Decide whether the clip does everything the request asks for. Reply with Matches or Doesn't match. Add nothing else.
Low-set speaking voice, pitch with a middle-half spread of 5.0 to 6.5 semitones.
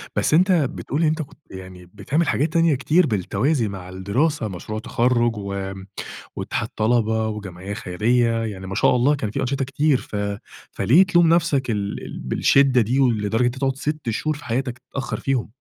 Matches